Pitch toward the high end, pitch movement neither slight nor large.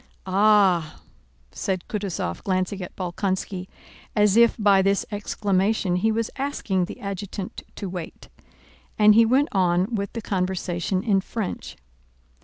No: high, 195 Hz; narrow, 2.3 semitones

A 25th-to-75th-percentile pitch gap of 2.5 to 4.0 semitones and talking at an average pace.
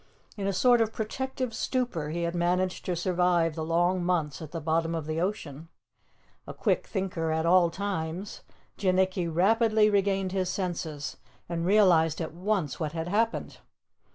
Yes: average, 3.3 semitones; average, 160 wpm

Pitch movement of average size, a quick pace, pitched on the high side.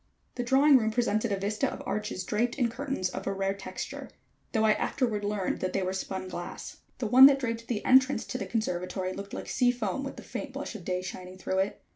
Yes: average, 4.6 semitones; fast, 225 wpm; high, 215 Hz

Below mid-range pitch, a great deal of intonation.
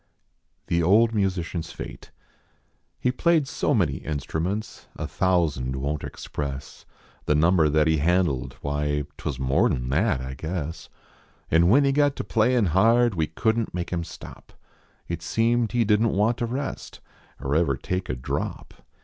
Yes: very low, 85 Hz; wide, 7.4 semitones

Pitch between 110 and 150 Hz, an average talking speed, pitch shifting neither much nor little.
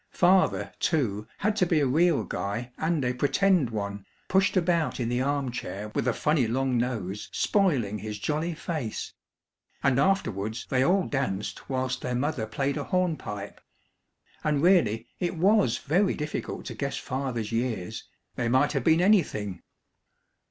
No: low, 135 Hz; average, 155 wpm; wide, 6.6 semitones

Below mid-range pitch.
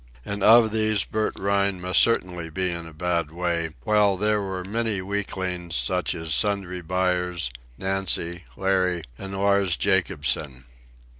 Yes: very low, 95 Hz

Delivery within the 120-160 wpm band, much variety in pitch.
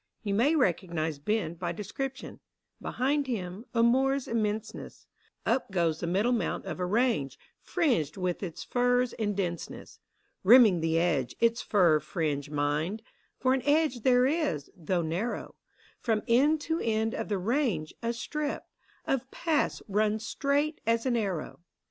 Yes: average, 155 wpm; wide, 6.5 semitones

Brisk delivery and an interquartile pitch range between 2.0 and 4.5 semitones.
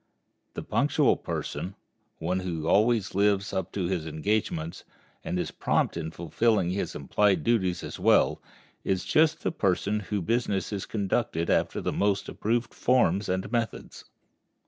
No: average, 145 wpm; average, 3.3 semitones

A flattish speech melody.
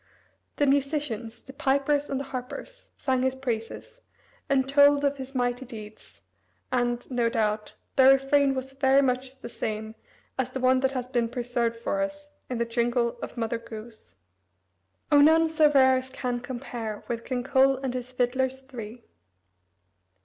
Yes: narrow, 2.3 semitones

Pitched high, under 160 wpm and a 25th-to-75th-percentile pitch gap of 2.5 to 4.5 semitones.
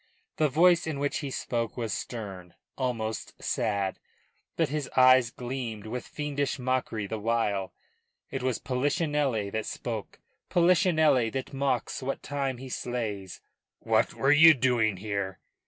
No: low, 125 Hz; average, 140 wpm; average, 4.2 semitones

